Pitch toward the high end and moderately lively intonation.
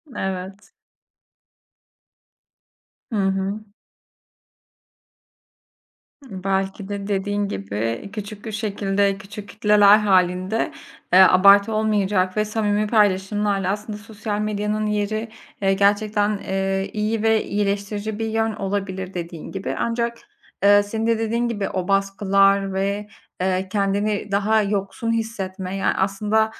No: high, 205 Hz; narrow, 1.7 semitones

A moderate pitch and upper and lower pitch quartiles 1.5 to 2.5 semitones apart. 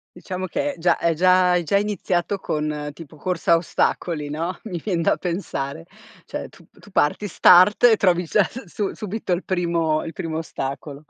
No: medium, 175 Hz; average, 2.9 semitones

